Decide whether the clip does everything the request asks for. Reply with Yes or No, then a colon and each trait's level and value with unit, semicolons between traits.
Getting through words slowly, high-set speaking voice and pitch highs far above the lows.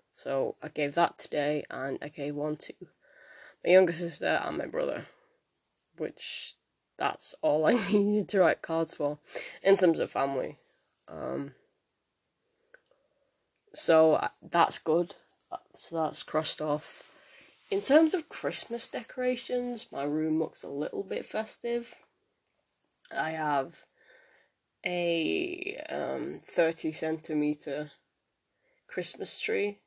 No: slow, 115 wpm; medium, 170 Hz; wide, 7.5 semitones